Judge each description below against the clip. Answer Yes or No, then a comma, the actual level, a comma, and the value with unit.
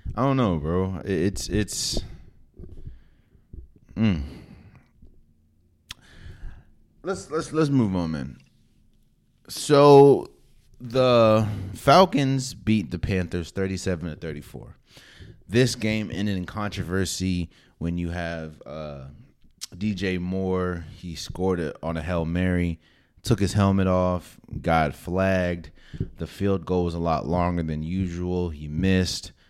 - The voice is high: No, very low, 90 Hz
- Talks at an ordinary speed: No, slow, 120 wpm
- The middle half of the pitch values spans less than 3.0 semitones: No, average, 3.5 semitones